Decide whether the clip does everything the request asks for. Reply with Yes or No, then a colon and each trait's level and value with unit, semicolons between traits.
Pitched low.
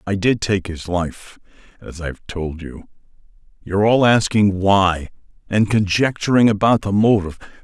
Yes: low, 100 Hz